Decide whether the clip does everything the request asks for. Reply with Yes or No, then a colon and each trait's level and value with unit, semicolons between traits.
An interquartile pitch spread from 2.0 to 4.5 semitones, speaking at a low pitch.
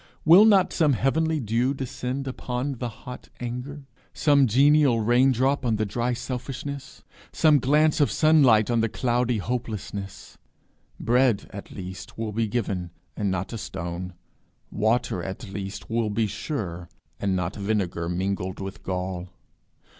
No: wide, 5.4 semitones; low, 115 Hz